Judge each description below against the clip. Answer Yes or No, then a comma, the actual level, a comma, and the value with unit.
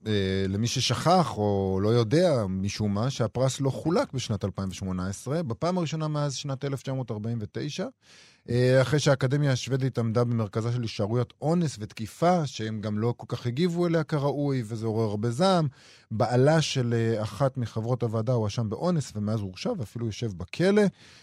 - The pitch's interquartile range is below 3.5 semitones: No, average, 4.6 semitones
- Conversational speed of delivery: Yes, average, 140 wpm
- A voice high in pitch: No, low, 120 Hz